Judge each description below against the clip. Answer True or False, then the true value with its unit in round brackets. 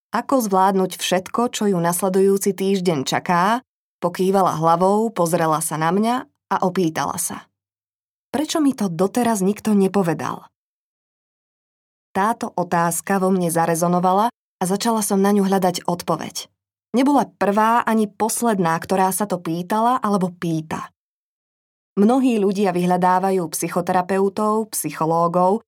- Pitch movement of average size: True (3.5 semitones)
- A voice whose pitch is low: False (190 Hz)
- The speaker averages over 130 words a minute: False (115 wpm)